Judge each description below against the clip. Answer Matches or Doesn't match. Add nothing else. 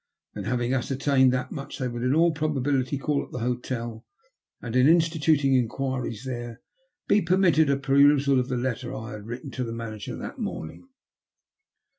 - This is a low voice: Matches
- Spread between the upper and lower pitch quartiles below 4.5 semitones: Matches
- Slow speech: Doesn't match